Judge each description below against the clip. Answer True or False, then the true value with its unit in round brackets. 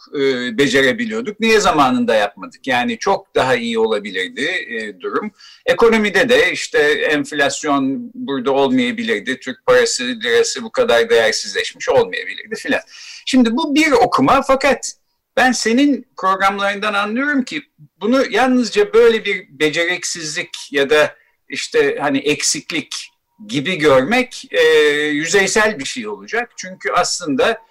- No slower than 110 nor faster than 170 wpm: True (115 wpm)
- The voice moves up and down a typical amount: False (7.9 semitones)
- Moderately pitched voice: False (245 Hz)